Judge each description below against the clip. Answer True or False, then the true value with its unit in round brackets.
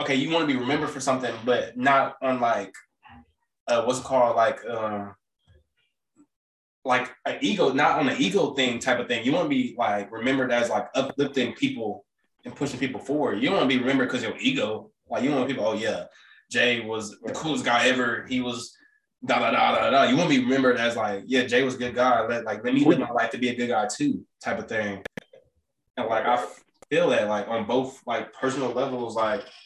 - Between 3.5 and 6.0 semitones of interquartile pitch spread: False (2.7 semitones)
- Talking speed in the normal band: False (225 wpm)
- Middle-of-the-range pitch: False (130 Hz)